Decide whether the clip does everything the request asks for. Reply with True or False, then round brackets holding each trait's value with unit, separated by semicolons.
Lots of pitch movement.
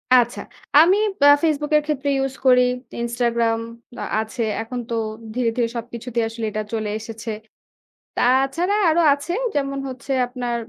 False (3.2 semitones)